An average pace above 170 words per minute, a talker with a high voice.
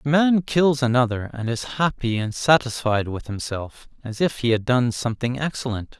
No: average, 180 wpm; low, 125 Hz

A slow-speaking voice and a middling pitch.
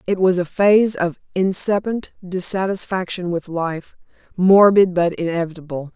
Yes: slow, 120 wpm; medium, 180 Hz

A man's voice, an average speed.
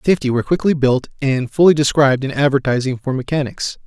Yes: male; average, 170 wpm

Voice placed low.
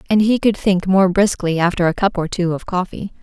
No: medium, 185 Hz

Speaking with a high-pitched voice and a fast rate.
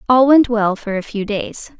Yes: high, 225 Hz; fast, 235 wpm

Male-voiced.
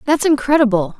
No: female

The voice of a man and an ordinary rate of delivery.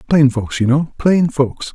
Yes: male; average, 170 wpm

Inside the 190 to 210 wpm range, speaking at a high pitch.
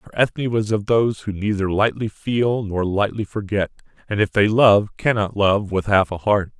No: average, 200 wpm; low, 105 Hz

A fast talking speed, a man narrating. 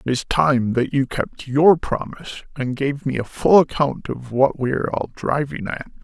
Yes: fast, 210 wpm; male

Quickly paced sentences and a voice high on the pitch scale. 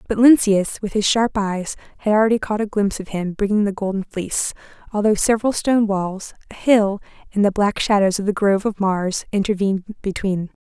No: average, 190 wpm; high, 205 Hz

